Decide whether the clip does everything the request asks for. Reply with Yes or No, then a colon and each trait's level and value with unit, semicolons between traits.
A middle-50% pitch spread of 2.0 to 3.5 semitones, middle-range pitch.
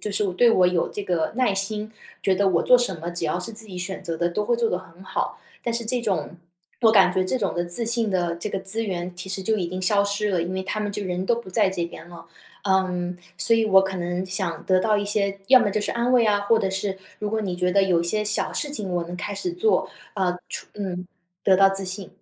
No: average, 2.8 semitones; high, 195 Hz